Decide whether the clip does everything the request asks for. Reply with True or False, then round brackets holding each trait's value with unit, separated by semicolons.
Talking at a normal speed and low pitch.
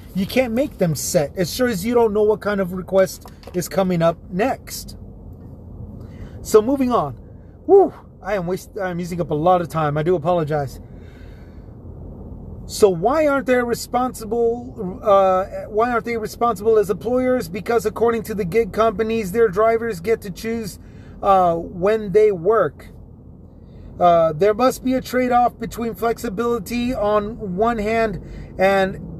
False (155 wpm; 205 Hz)